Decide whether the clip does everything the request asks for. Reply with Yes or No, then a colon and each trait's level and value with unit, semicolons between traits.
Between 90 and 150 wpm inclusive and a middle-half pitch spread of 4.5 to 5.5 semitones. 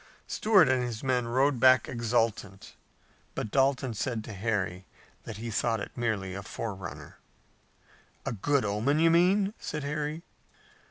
Yes: average, 145 wpm; average, 4.8 semitones